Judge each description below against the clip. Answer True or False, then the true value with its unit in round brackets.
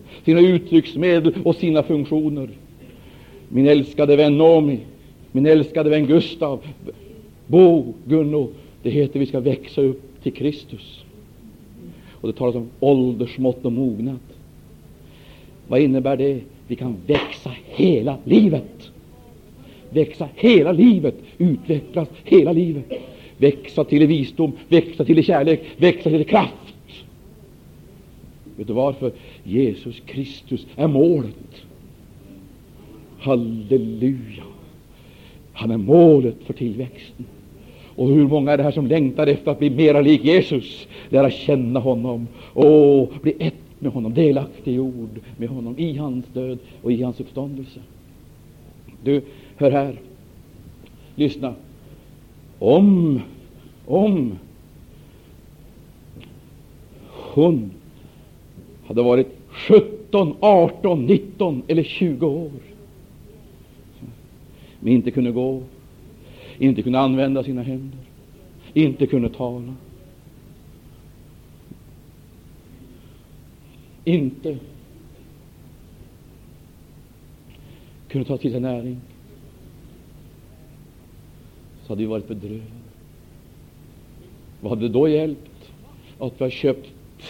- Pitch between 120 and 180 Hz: True (135 Hz)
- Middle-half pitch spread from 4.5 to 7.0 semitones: False (3.5 semitones)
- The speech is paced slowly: True (100 wpm)